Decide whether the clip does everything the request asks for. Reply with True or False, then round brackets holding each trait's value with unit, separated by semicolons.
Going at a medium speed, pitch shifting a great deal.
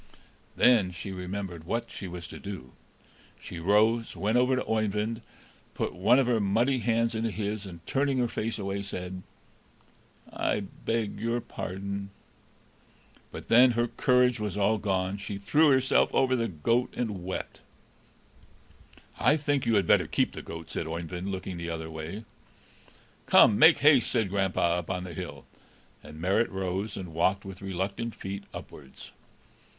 False (160 wpm; 4.0 semitones)